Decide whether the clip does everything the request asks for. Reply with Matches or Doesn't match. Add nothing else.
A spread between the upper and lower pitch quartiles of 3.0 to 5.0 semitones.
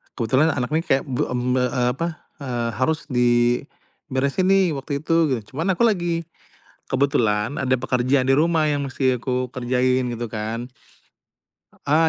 Matches